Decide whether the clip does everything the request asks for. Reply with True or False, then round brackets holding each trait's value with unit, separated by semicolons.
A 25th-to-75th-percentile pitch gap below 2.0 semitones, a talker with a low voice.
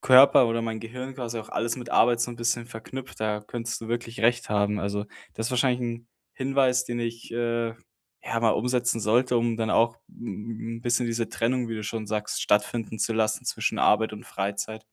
True (1.5 semitones; 115 Hz)